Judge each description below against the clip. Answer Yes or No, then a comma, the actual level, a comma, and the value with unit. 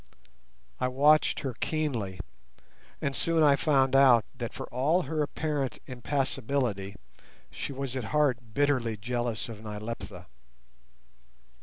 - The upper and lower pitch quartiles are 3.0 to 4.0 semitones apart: Yes, average, 3.7 semitones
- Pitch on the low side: Yes, low, 130 Hz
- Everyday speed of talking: No, slow, 120 wpm